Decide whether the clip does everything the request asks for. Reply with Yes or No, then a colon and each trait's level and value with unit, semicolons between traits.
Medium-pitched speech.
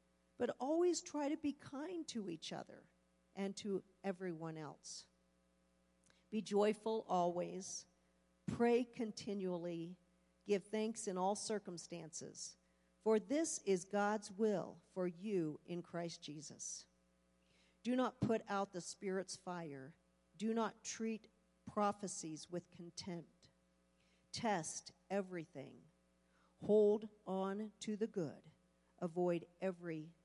Yes: medium, 180 Hz